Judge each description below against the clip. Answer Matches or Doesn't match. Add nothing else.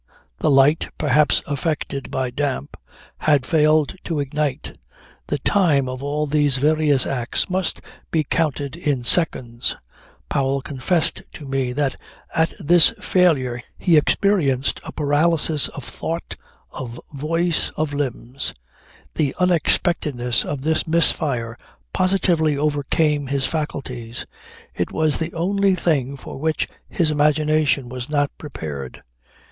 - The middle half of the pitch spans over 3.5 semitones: Doesn't match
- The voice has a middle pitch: Matches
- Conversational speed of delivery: Doesn't match